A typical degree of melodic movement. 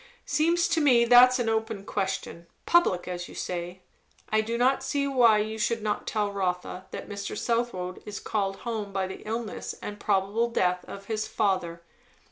Yes: average, 3.7 semitones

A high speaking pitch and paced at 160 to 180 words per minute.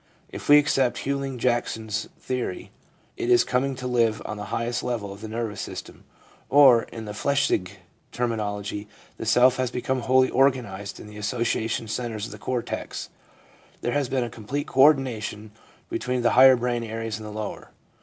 No: low, 120 Hz; average, 175 wpm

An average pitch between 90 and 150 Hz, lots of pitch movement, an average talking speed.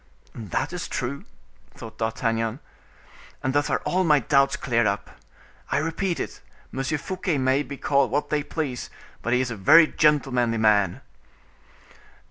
No: low, 135 Hz; average, 4.6 semitones; average, 150 wpm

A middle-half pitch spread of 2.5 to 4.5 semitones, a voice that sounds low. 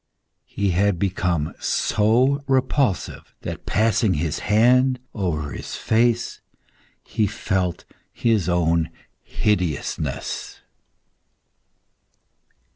No: average, 5.0 semitones; low, 100 Hz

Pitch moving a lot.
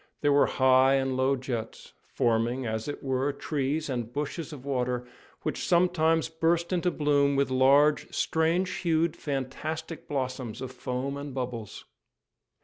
No: average, 3.5 semitones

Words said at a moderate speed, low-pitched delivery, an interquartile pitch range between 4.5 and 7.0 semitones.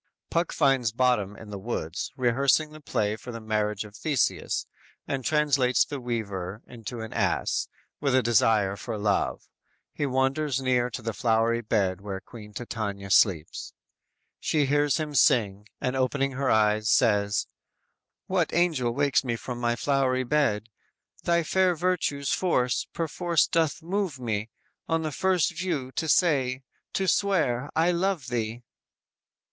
Yes: average, 150 wpm; low, 125 Hz; wide, 5.4 semitones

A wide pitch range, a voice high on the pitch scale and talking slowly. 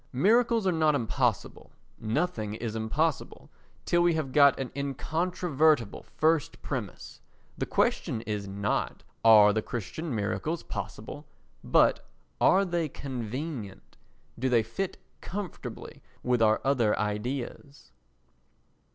No: wide, 6.4 semitones; low, 135 Hz; slow, 115 wpm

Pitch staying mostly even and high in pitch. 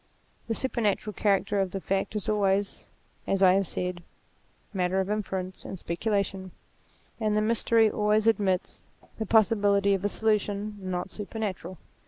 Yes: narrow, 2.0 semitones; high, 200 Hz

